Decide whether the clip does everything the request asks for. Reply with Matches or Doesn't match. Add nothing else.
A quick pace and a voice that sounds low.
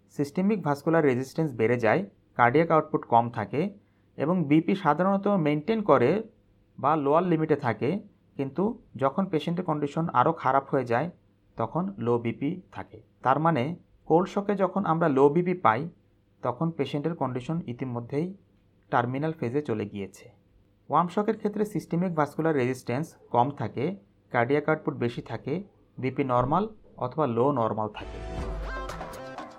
Doesn't match